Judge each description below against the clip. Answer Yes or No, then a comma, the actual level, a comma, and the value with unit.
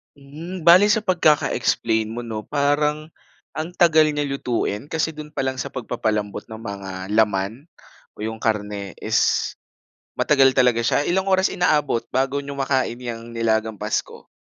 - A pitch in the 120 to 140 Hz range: Yes, low, 135 Hz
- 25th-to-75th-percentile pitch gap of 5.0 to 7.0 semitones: Yes, average, 5.3 semitones